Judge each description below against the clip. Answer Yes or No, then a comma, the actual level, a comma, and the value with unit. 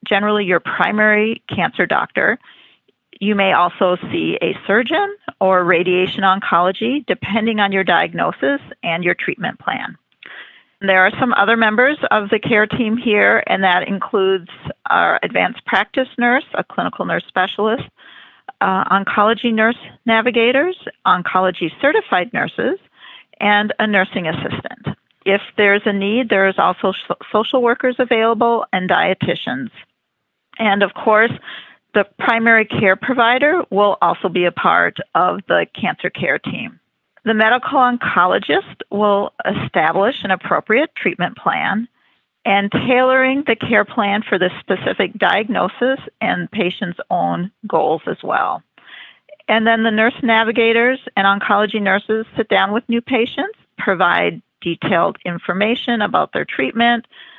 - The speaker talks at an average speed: No, slow, 130 wpm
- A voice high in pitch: Yes, high, 215 Hz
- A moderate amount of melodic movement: Yes, average, 3.5 semitones